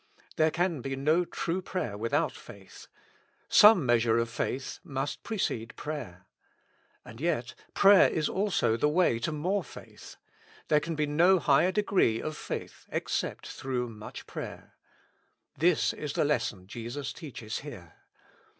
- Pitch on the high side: No, medium, 145 Hz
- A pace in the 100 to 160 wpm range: Yes, average, 140 wpm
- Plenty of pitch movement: Yes, wide, 6.4 semitones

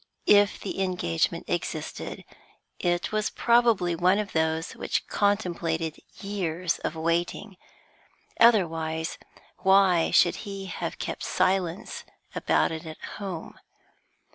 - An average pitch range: Yes, average, 3.4 semitones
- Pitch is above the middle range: No, medium, 180 Hz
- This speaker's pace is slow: Yes, slow, 110 wpm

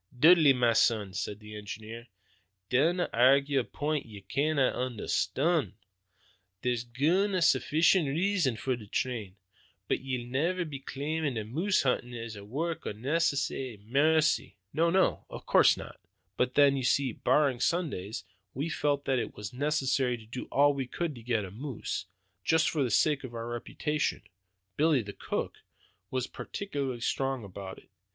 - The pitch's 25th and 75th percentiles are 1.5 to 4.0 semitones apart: No, average, 4.5 semitones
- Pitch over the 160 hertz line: No, low, 135 Hz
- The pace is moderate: Yes, average, 165 wpm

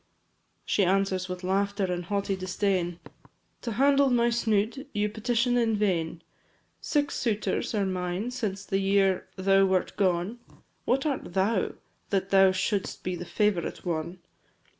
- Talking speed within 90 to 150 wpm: Yes, average, 145 wpm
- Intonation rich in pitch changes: No, average, 3.1 semitones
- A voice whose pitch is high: Yes, high, 195 Hz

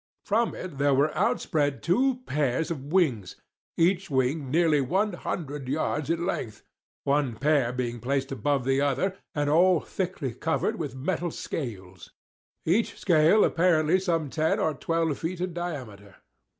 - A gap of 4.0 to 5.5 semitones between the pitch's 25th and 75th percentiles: Yes, average, 4.5 semitones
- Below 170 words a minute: Yes, average, 140 wpm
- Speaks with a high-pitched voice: No, medium, 150 Hz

